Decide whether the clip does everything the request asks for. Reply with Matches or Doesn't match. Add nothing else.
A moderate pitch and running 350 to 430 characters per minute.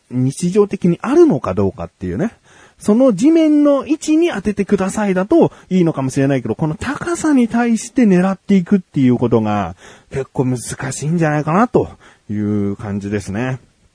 Matches